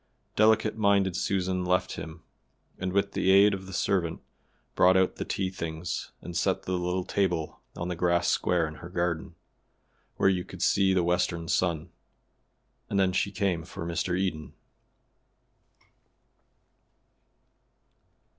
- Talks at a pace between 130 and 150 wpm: Yes, average, 140 wpm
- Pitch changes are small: Yes, narrow, 2.1 semitones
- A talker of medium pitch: No, very low, 90 Hz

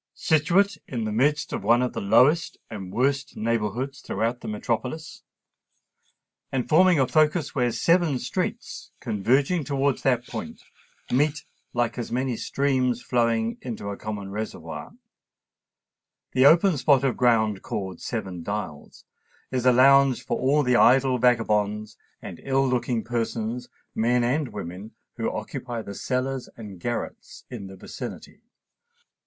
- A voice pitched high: No, low, 125 Hz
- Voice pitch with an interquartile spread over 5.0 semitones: No, average, 3.8 semitones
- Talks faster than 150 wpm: No, average, 140 wpm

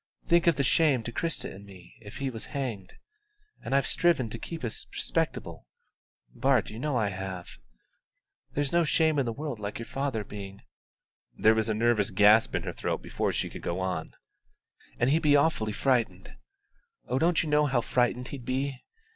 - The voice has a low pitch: Yes, low, 120 Hz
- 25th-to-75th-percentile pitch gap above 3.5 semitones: Yes, average, 5.2 semitones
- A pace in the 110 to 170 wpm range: No, average, 195 wpm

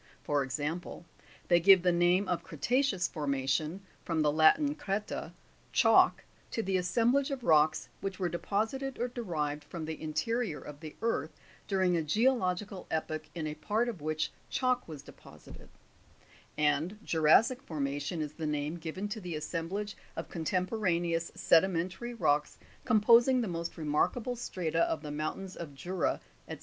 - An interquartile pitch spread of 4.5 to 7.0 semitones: Yes, average, 5.2 semitones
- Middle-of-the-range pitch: Yes, medium, 175 Hz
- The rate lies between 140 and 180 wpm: Yes, average, 155 wpm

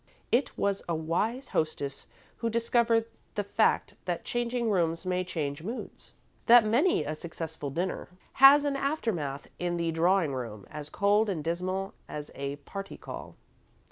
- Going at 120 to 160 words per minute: Yes, average, 150 wpm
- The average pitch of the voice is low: No, medium, 185 Hz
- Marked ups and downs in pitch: Yes, wide, 6.4 semitones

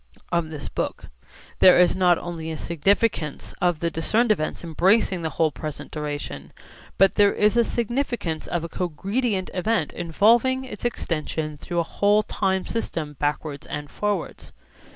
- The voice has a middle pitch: Yes, medium, 175 Hz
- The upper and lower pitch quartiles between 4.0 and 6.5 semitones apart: Yes, average, 4.8 semitones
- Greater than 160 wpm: No, average, 155 wpm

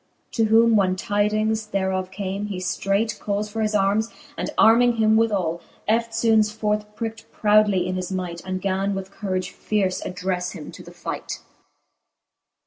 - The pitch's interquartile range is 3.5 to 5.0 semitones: No, narrow, 2.6 semitones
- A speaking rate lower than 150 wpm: No, average, 155 wpm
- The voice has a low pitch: No, high, 205 Hz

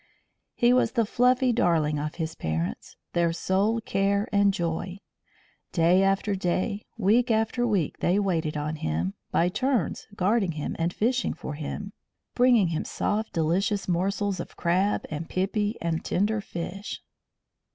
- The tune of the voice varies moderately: Yes, average, 4.2 semitones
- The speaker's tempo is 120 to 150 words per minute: Yes, average, 145 wpm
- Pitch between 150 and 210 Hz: Yes, high, 190 Hz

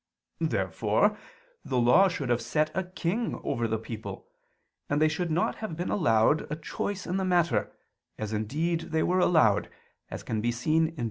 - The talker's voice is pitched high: No, medium, 155 Hz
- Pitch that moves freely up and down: Yes, wide, 6.9 semitones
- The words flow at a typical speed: Yes, average, 155 wpm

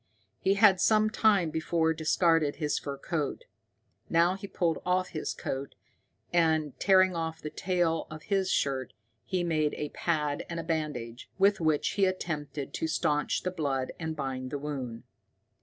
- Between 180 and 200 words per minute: No, average, 160 wpm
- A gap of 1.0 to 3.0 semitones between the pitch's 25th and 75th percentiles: No, average, 3.5 semitones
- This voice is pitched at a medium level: Yes, medium, 160 Hz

